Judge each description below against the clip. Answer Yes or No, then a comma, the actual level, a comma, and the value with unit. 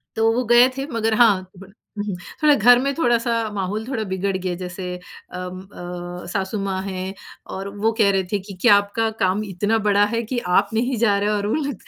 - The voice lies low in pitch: No, high, 205 Hz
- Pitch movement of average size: Yes, average, 3.3 semitones